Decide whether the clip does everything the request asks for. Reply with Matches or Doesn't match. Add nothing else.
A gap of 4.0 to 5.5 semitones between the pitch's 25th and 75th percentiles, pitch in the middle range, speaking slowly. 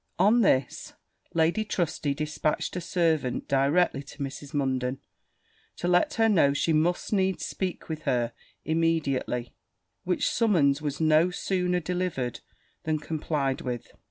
Matches